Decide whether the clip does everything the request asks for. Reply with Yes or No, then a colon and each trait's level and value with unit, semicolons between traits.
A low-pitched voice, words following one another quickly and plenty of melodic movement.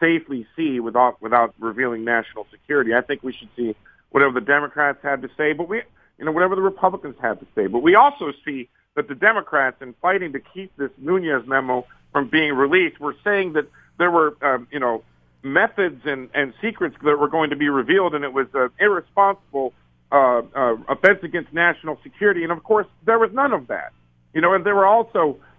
No: medium, 150 Hz; fast, 210 wpm; wide, 6.5 semitones